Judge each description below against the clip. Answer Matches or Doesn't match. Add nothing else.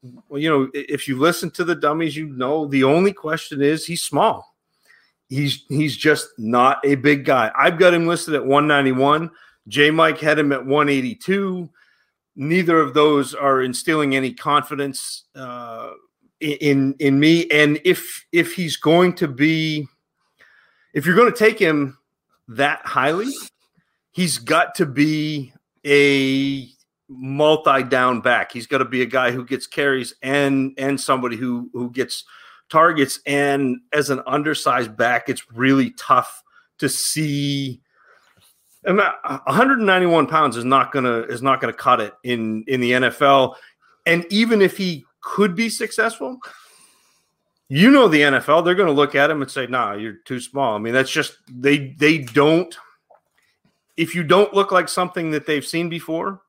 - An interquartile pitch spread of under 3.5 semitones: Doesn't match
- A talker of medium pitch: Matches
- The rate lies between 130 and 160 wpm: Matches